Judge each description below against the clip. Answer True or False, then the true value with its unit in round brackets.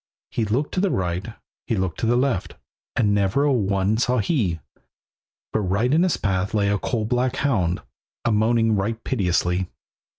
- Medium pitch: False (110 Hz)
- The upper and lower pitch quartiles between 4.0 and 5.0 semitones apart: True (4.3 semitones)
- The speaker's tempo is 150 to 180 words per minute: True (175 wpm)